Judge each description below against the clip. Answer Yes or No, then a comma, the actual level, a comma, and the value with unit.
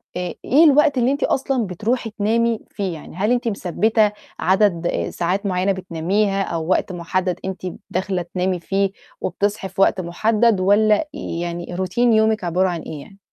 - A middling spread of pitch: Yes, average, 3.3 semitones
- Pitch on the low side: No, high, 195 Hz